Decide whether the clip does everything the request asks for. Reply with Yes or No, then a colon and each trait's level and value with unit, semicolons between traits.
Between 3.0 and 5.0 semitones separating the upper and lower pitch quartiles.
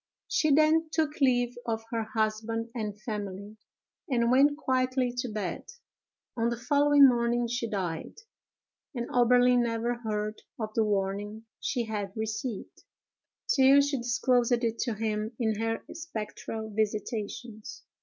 No: narrow, 2.6 semitones